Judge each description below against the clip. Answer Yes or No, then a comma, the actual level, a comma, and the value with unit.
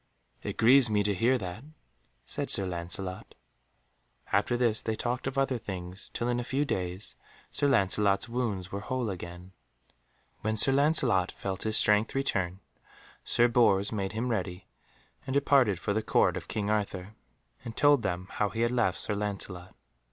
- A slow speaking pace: No, average, 165 wpm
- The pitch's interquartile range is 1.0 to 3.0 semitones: No, average, 4.2 semitones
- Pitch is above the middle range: No, low, 105 Hz